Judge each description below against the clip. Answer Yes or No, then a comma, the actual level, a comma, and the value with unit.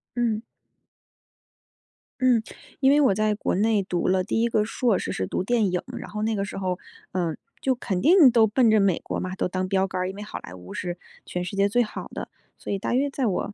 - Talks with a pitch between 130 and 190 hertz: No, high, 205 Hz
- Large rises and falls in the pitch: No, average, 4.1 semitones